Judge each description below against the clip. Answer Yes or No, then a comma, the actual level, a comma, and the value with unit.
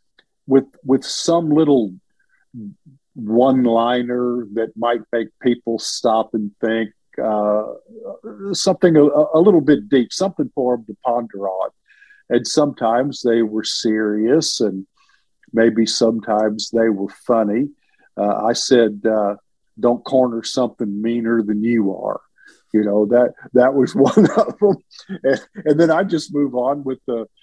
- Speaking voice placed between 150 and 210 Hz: No, low, 120 Hz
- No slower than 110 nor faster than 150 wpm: Yes, average, 140 wpm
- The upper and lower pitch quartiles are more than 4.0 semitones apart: Yes, average, 4.7 semitones